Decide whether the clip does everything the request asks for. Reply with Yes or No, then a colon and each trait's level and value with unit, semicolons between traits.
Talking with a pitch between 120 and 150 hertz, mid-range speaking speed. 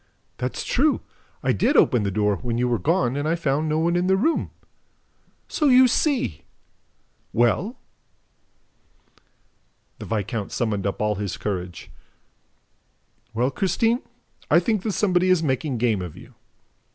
Yes: low, 135 Hz; average, 145 wpm